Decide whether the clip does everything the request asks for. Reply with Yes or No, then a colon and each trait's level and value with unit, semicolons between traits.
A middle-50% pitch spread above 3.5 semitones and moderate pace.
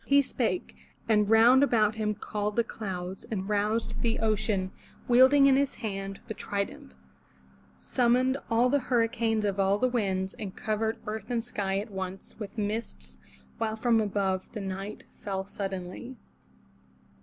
No: average, 3.2 semitones; average, 155 wpm